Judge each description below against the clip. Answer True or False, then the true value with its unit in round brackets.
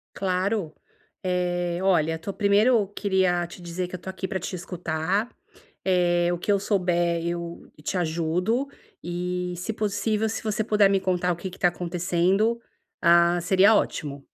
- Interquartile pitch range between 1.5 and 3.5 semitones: True (2.5 semitones)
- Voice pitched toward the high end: False (180 Hz)